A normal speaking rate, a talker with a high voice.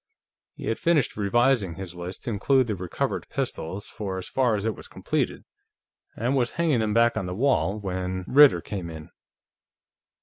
No: average, 175 wpm; low, 105 Hz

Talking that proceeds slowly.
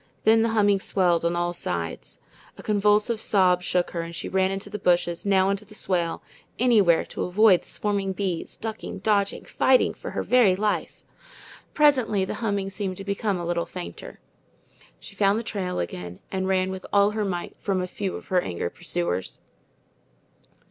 No: average, 180 wpm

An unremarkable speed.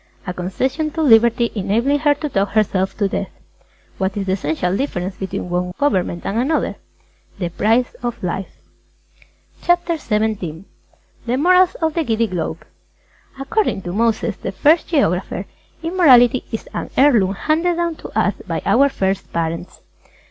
Yes: average, 165 wpm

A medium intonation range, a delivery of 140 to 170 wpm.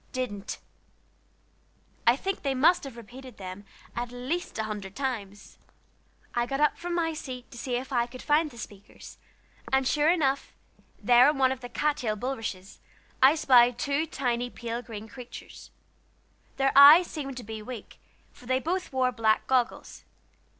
Yes: average, 3.1 semitones; average, 165 wpm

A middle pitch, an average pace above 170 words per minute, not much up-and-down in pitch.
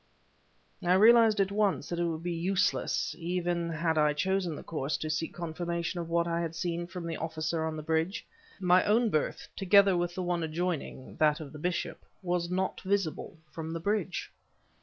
Yes: medium, 170 Hz; average, 190 wpm; narrow, 2.3 semitones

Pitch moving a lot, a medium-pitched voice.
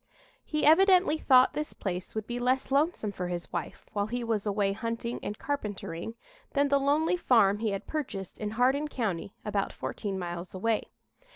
No: wide, 6.0 semitones; high, 225 Hz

